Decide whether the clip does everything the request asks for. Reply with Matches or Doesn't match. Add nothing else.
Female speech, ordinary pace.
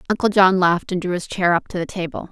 Doesn't match